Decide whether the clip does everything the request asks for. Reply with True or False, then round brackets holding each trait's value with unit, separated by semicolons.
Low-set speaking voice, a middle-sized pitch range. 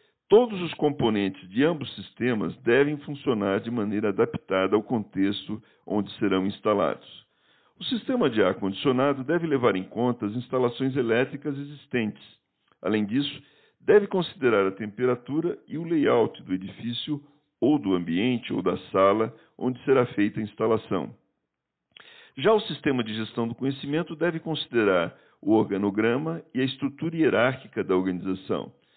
False (125 Hz; 6.1 semitones)